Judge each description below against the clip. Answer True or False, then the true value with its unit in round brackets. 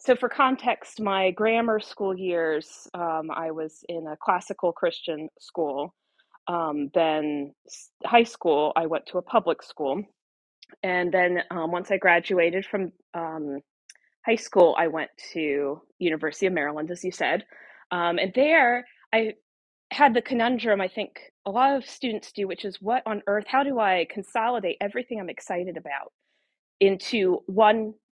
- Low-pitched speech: False (190 Hz)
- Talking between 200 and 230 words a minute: False (160 wpm)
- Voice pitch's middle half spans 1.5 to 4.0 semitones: False (5.2 semitones)